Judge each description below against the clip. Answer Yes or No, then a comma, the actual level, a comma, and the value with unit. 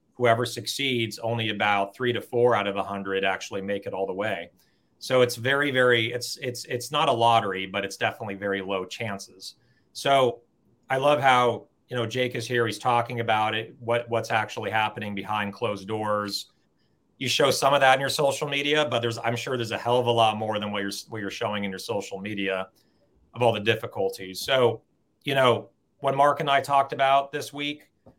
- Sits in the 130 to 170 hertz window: No, low, 115 Hz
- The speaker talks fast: Yes, fast, 210 wpm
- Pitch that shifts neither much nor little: Yes, average, 3.6 semitones